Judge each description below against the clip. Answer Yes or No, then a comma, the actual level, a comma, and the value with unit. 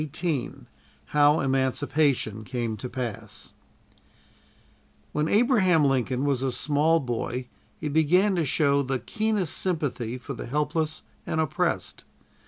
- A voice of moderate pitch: Yes, medium, 145 Hz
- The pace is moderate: No, slow, 125 wpm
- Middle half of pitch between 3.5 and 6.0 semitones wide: Yes, average, 3.8 semitones